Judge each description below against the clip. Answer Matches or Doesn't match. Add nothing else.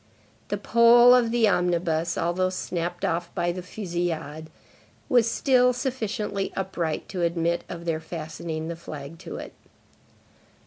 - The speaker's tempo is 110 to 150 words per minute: Matches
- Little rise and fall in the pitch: Doesn't match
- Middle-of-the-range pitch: Matches